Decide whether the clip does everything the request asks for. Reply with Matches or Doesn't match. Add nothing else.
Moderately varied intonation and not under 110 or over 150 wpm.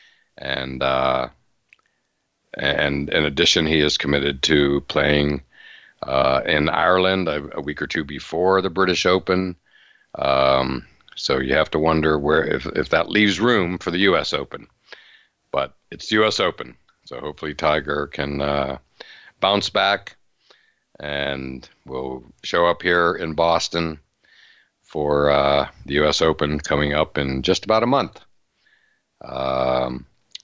Matches